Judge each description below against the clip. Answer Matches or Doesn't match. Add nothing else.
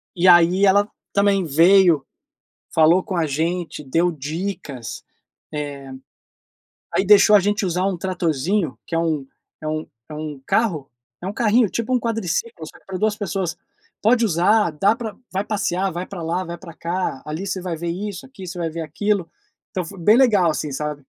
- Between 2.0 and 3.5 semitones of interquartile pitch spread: Doesn't match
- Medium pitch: Matches